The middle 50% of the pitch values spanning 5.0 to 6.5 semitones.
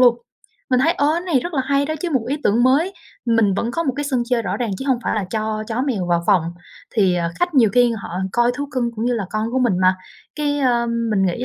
No: average, 4.4 semitones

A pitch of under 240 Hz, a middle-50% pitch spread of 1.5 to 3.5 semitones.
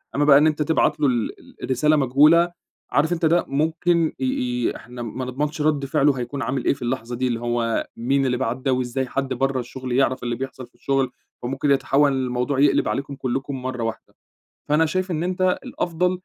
Yes: low, 135 Hz; average, 3.2 semitones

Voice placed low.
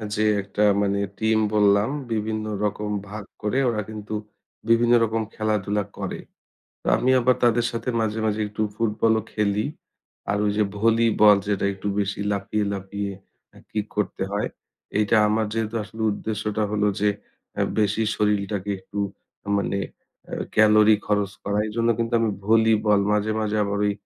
Yes: low, 105 Hz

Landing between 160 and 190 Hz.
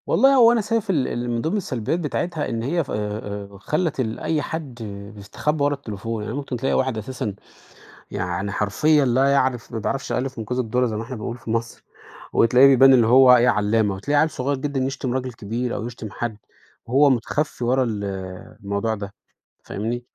No: low, 125 Hz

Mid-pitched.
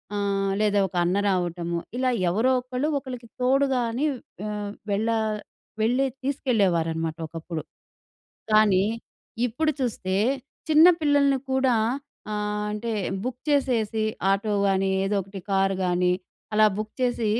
No: high, 215 Hz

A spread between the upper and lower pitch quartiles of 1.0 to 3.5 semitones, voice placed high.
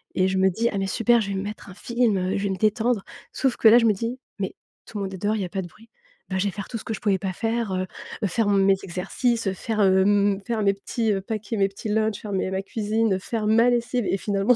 Yes: average, 2.8 semitones; high, 205 Hz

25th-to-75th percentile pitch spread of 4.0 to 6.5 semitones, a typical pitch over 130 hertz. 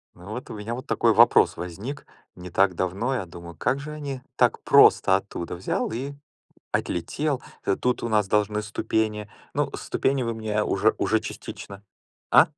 No: average, 4.8 semitones; low, 105 Hz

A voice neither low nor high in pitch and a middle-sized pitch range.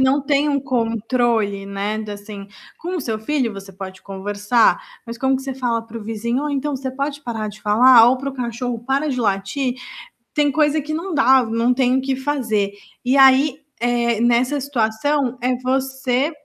No: very high, 250 Hz; average, 3.6 semitones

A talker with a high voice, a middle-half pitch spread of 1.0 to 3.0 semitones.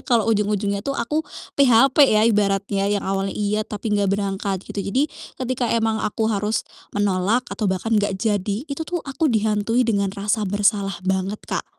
Yes: high, 210 Hz; narrow, 2.5 semitones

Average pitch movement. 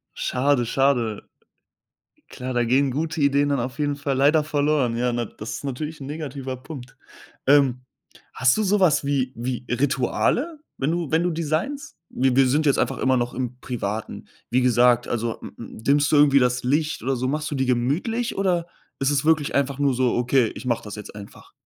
Yes: average, 3.2 semitones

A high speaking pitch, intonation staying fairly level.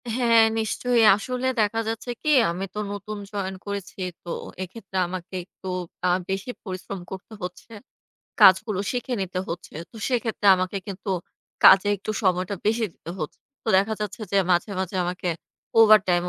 No: high, 200 Hz; average, 3.2 semitones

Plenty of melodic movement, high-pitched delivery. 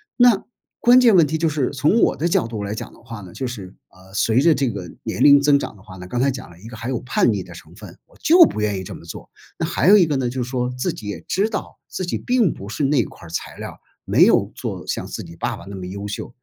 No: wide, 7.4 semitones; low, 125 Hz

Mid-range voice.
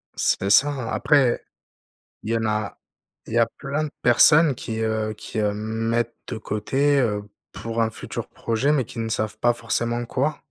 No: low, 115 Hz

